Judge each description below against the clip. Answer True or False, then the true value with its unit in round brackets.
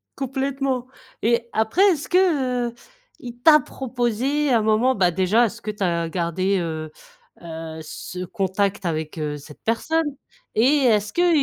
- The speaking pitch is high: True (225 Hz)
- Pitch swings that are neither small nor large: False (6.8 semitones)